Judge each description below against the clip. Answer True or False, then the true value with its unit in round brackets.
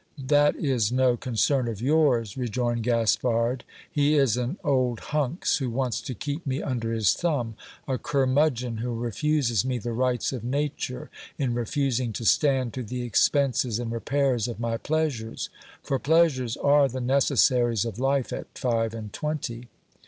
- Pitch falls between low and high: False (125 Hz)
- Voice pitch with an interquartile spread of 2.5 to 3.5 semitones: True (3.1 semitones)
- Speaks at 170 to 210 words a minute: False (160 wpm)